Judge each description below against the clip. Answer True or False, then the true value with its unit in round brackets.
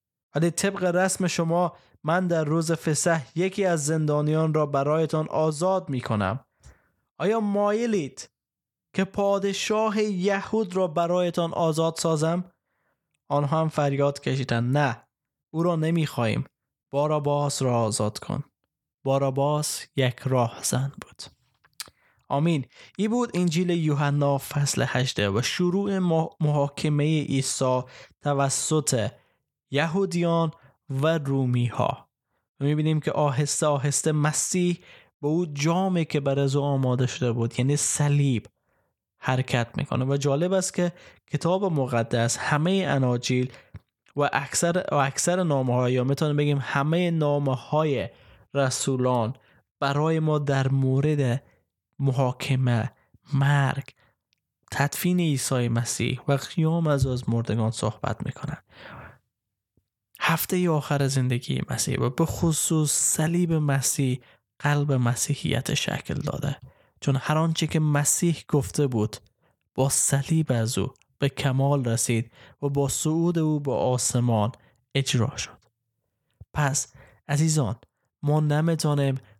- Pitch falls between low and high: True (145 Hz)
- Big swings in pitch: False (3.8 semitones)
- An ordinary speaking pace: True (115 wpm)